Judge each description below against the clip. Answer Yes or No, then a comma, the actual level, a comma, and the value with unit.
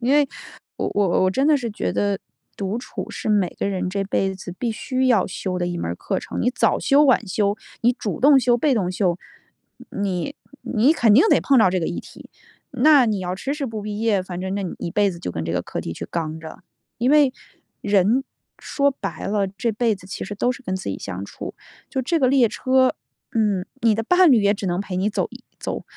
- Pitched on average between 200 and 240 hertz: Yes, high, 210 Hz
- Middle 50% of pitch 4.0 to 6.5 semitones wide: Yes, average, 5.2 semitones